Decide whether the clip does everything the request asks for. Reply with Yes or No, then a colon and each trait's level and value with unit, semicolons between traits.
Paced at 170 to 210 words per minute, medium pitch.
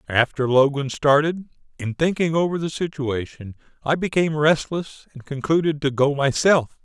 No: average, 140 wpm; medium, 145 Hz